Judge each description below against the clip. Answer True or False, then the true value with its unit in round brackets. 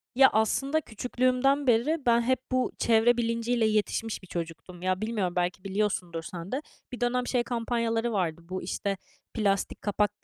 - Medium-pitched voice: False (225 Hz)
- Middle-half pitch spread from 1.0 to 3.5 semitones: False (4.4 semitones)